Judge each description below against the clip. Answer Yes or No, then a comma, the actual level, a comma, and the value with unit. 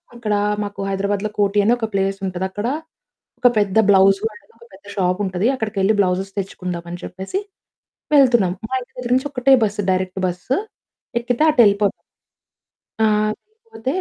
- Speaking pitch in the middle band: No, high, 205 Hz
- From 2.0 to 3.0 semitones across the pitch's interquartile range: No, average, 3.8 semitones